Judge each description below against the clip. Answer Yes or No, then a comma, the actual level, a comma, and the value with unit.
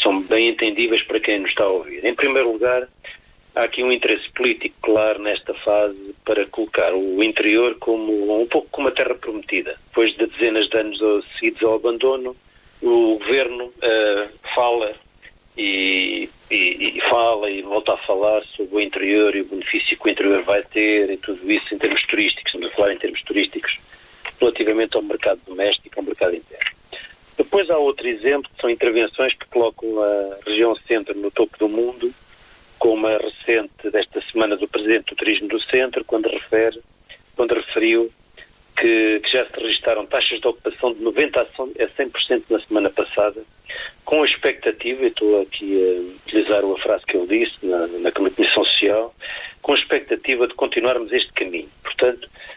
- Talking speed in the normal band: Yes, average, 170 wpm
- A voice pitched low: Yes, low, 115 Hz